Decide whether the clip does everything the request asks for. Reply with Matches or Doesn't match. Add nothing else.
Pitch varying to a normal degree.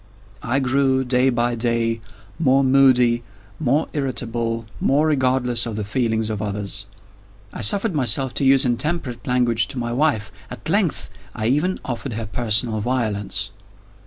Matches